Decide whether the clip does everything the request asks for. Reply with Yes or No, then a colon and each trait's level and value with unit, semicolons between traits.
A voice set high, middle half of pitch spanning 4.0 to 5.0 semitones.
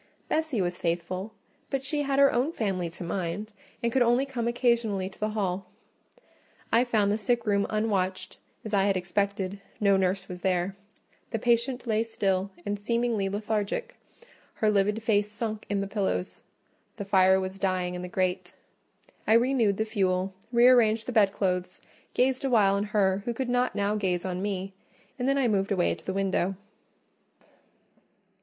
No: high, 205 Hz; average, 3.6 semitones